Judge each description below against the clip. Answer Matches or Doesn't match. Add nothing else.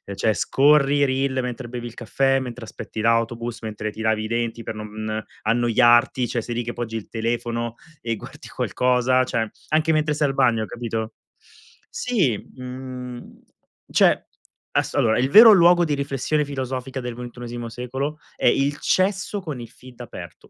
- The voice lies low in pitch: Matches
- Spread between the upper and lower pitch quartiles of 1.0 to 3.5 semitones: Matches